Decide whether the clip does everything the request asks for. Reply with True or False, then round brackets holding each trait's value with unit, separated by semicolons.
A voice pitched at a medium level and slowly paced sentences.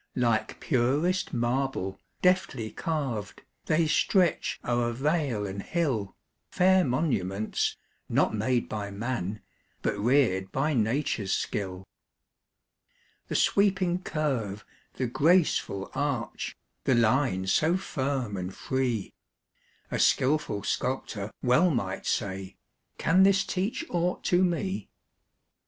False (130 Hz; 110 wpm)